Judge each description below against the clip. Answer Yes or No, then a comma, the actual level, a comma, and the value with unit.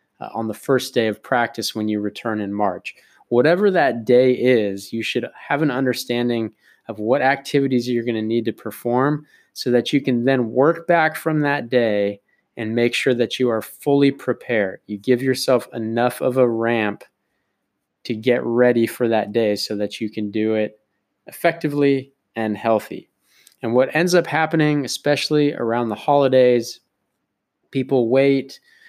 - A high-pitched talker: No, low, 120 Hz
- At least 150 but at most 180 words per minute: Yes, average, 170 wpm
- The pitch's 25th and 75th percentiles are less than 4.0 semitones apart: Yes, average, 3.5 semitones